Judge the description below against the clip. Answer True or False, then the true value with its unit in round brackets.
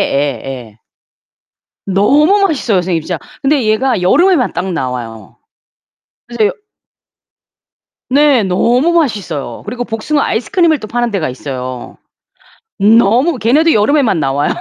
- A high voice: True (215 Hz)